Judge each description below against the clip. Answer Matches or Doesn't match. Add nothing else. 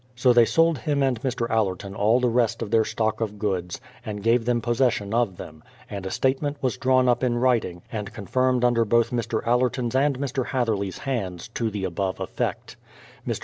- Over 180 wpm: Matches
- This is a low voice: Matches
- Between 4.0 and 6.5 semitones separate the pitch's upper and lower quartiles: Doesn't match